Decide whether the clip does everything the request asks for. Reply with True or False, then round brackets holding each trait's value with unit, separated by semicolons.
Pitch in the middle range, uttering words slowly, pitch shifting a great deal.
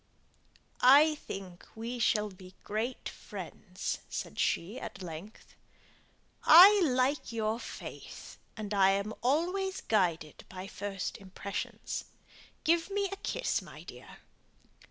False (220 Hz; 115 wpm; 7.6 semitones)